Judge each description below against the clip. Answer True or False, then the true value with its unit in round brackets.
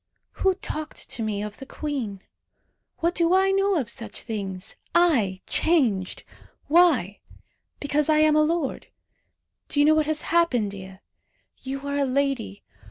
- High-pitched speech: True (280 Hz)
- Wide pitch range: True (7.0 semitones)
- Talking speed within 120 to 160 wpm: True (155 wpm)